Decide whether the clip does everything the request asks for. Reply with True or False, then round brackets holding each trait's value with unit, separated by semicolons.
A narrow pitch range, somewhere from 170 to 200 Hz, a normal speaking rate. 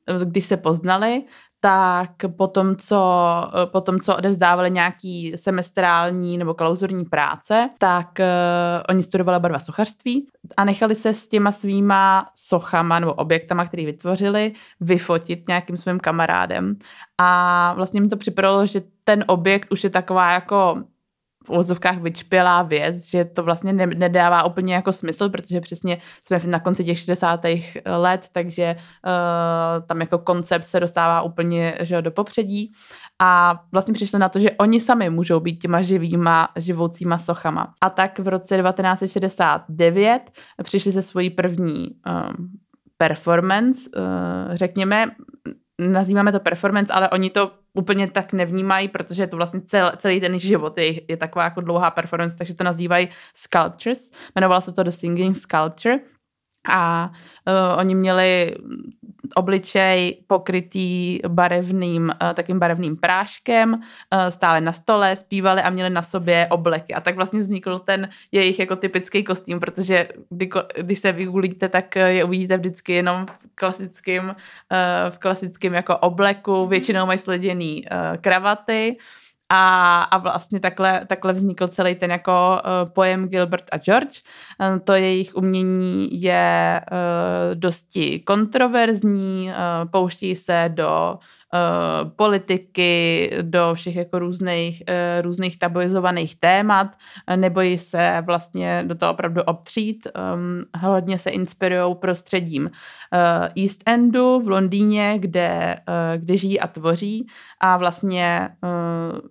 True (1.8 semitones; 185 Hz; 130 wpm)